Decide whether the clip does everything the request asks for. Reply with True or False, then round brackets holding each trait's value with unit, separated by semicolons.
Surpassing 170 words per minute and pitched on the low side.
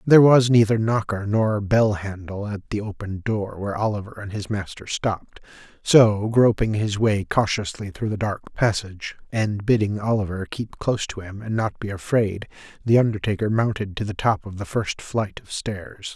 True (180 wpm; 105 Hz)